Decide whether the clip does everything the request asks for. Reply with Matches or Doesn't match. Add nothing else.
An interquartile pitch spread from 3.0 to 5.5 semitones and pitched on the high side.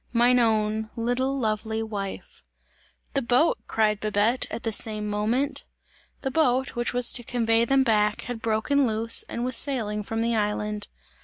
Doesn't match